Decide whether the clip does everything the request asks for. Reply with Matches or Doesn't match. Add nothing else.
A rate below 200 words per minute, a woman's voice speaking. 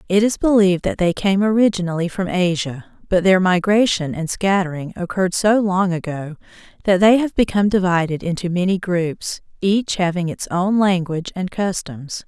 Matches